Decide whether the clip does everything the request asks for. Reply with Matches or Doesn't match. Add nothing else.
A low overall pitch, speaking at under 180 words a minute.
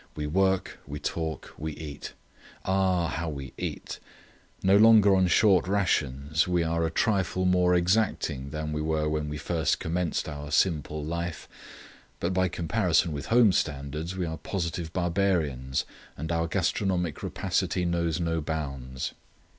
Matches